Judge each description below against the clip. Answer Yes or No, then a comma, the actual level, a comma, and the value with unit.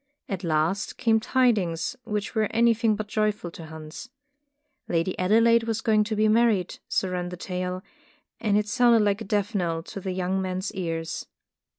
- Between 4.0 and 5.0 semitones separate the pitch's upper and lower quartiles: No, average, 3.4 semitones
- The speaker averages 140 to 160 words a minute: No, average, 175 wpm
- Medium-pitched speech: No, high, 200 Hz